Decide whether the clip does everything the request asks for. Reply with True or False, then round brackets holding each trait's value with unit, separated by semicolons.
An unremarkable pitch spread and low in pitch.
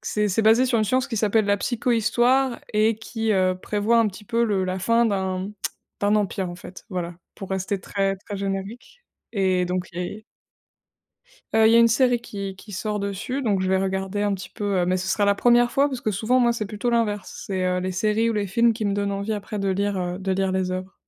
False (3.1 semitones; 205 Hz)